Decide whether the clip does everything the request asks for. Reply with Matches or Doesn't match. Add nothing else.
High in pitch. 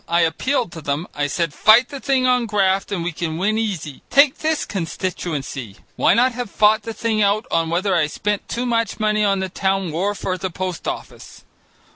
Matches